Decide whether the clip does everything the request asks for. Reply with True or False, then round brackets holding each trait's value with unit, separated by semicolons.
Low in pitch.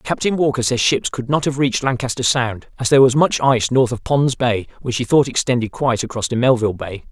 True (125 Hz)